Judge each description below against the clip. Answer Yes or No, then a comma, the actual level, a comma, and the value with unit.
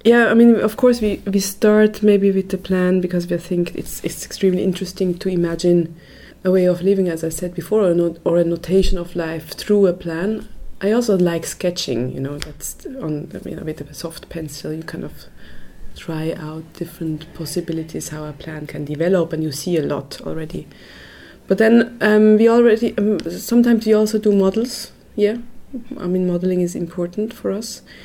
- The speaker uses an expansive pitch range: No, average, 4.2 semitones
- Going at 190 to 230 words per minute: Yes, average, 200 wpm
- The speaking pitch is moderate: Yes, medium, 180 Hz